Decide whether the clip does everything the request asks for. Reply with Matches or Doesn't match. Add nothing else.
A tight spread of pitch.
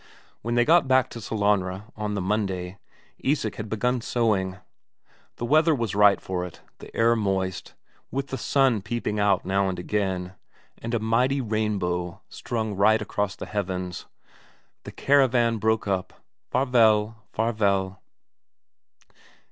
Doesn't match